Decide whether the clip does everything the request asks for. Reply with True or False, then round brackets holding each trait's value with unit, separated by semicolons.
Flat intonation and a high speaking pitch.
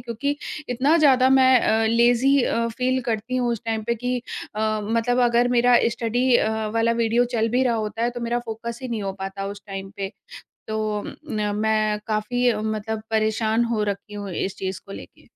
True (2.3 semitones; 230 Hz)